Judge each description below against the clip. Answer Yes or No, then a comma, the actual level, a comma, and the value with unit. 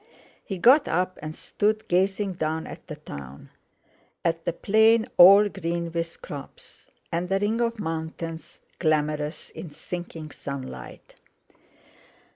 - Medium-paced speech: No, slow, 125 wpm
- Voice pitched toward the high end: No, medium, 170 Hz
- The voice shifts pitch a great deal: No, average, 4.1 semitones